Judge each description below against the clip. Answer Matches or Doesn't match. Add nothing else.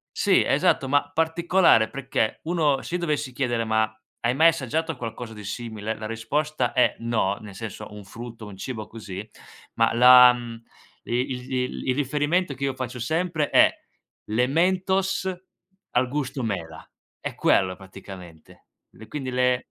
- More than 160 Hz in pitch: Doesn't match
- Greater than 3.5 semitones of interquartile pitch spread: Matches